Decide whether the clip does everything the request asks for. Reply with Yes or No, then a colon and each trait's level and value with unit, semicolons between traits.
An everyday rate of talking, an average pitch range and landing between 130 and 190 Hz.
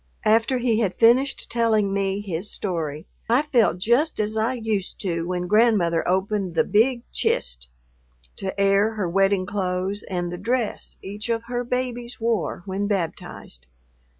No: average, 150 wpm; average, 4.0 semitones; high, 205 Hz